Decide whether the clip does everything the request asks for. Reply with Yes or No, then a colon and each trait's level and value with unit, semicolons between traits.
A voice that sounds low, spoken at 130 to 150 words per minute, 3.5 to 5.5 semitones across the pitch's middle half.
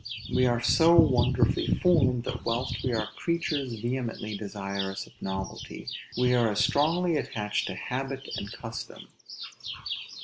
Yes: low, 125 Hz; slow, 135 wpm; average, 3.9 semitones